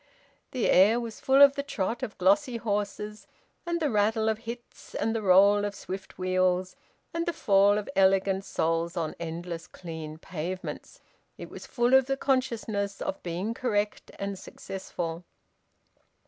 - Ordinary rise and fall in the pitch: Yes, average, 4.0 semitones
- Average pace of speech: Yes, average, 155 wpm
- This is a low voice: No, high, 200 Hz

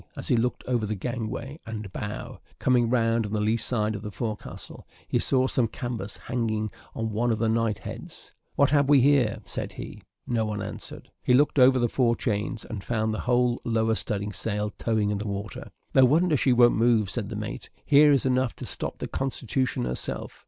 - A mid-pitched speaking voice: No, low, 115 Hz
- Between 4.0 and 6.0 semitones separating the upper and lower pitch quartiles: No, average, 2.8 semitones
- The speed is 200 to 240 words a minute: Yes, fast, 205 wpm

